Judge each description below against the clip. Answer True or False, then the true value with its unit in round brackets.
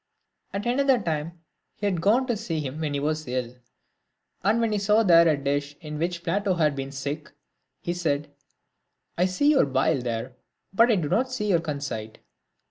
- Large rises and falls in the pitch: True (6.2 semitones)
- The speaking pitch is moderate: True (165 Hz)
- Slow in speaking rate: False (195 wpm)